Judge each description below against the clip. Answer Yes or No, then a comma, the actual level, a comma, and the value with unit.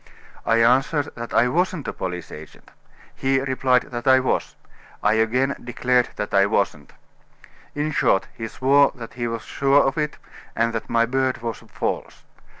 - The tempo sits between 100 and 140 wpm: No, average, 165 wpm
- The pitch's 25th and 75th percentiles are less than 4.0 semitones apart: Yes, average, 2.9 semitones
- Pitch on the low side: Yes, low, 125 Hz